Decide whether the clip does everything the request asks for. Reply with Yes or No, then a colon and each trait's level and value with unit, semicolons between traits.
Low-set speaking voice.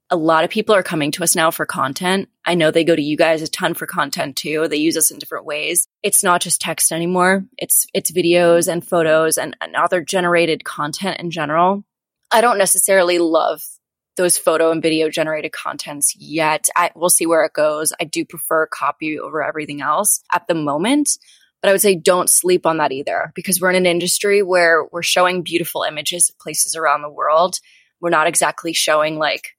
No: medium, 170 Hz